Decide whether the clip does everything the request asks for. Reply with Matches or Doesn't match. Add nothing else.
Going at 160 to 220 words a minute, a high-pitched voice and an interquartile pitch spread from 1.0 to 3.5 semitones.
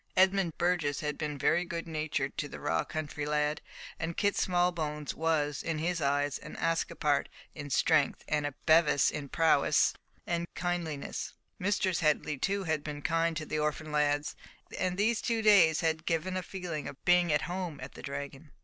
Doesn't match